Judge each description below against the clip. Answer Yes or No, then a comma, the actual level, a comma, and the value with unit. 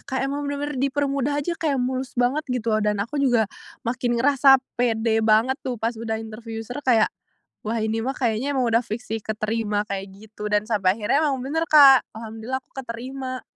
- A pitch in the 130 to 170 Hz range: No, high, 240 Hz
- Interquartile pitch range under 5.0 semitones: Yes, average, 3.5 semitones